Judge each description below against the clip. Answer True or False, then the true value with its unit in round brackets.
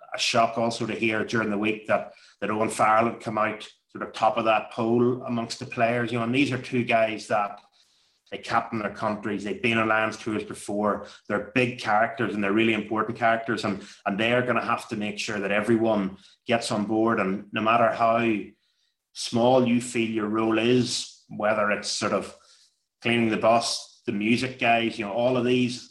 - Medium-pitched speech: False (115 Hz)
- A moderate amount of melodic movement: False (1.7 semitones)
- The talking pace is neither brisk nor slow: False (210 wpm)